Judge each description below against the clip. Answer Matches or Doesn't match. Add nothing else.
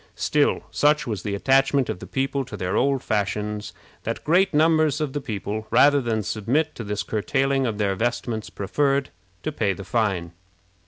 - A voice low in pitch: Matches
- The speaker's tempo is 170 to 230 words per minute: Matches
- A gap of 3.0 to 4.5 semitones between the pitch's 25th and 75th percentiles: Doesn't match